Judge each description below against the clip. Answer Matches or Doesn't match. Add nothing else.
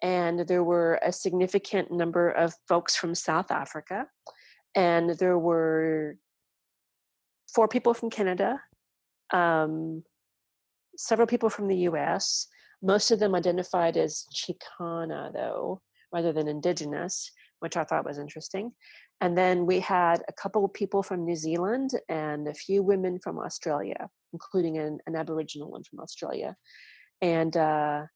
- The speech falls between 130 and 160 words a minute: Matches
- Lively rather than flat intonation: Doesn't match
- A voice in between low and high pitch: Matches